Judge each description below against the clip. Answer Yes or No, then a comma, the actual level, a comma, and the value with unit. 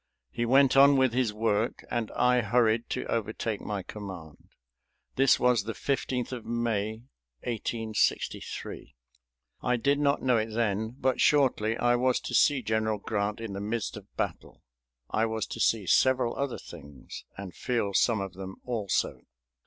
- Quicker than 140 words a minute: Yes, average, 160 wpm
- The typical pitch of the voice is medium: No, low, 115 Hz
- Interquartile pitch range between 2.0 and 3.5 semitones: Yes, average, 2.9 semitones